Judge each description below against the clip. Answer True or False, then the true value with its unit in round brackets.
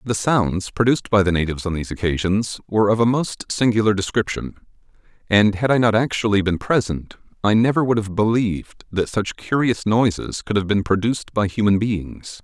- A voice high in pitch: False (105 Hz)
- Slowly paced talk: False (185 wpm)